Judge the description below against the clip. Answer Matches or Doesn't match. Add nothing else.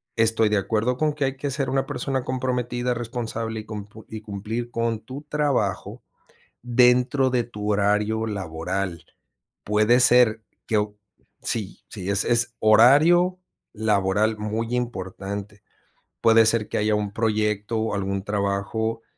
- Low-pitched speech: Matches